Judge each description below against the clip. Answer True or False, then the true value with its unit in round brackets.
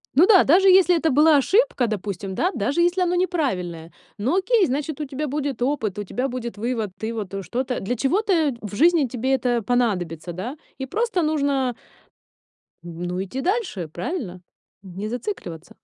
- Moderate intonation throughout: False (7.9 semitones)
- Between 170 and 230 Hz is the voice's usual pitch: False (260 Hz)